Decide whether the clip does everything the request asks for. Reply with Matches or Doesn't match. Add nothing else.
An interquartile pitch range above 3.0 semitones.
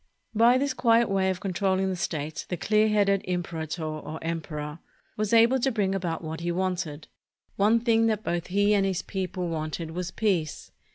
Matches